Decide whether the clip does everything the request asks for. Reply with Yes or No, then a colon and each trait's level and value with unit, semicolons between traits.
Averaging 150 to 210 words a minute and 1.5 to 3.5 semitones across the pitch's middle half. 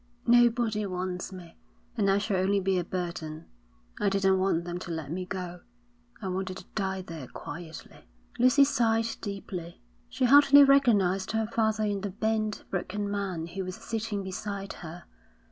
Yes: average, 160 wpm; average, 3.2 semitones